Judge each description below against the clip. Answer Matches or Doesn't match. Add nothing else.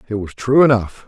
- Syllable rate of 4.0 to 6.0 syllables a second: Matches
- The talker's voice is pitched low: Matches